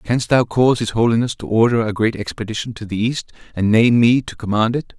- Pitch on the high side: No, low, 115 Hz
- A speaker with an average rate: No, fast, 230 wpm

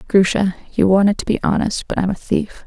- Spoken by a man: No, female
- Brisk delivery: Yes, fast, 225 wpm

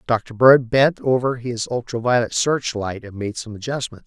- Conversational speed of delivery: Yes, average, 190 wpm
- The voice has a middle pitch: No, low, 120 Hz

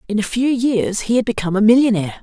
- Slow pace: No, fast, 245 wpm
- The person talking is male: No, female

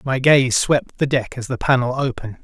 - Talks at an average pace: No, fast, 220 wpm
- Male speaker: Yes, male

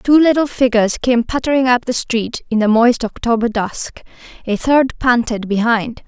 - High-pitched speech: Yes, high, 240 Hz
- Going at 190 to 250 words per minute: No, average, 170 wpm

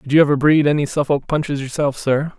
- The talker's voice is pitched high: No, medium, 145 Hz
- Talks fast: Yes, fast, 225 wpm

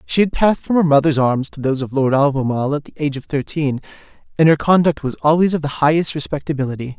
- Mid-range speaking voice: Yes, medium, 150 Hz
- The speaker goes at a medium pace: No, fast, 225 wpm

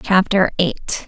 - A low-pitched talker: No, medium, 185 Hz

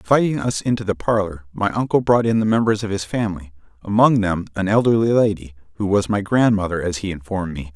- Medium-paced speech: No, fast, 210 wpm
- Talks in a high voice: No, low, 100 Hz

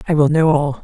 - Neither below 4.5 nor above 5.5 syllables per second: No, 6.0 syllables/s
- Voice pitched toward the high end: No, medium, 150 Hz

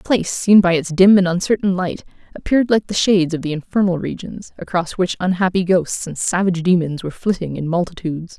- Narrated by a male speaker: No, female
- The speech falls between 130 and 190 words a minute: No, average, 200 wpm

